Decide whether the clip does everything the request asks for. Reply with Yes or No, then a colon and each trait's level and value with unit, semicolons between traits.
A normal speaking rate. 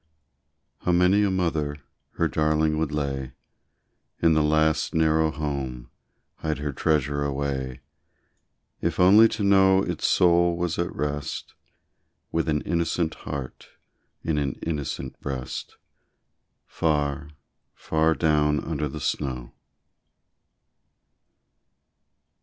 No: slow, 105 wpm